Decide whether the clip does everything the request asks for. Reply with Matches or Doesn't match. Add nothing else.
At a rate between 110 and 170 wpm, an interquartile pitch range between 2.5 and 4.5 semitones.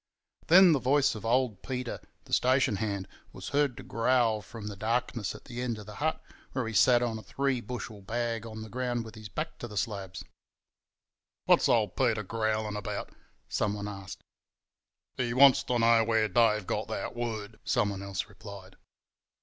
Doesn't match